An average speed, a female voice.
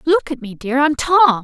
No: fast, 210 wpm; female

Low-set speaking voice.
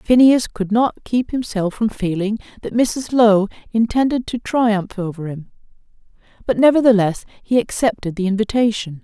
No: high, 220 Hz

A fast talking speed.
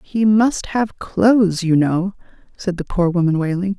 No: average, 175 wpm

